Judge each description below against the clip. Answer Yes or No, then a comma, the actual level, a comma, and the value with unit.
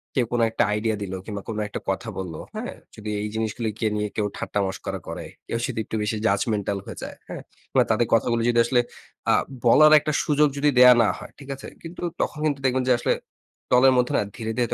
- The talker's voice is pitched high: No, low, 115 Hz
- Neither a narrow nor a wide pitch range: Yes, average, 3.4 semitones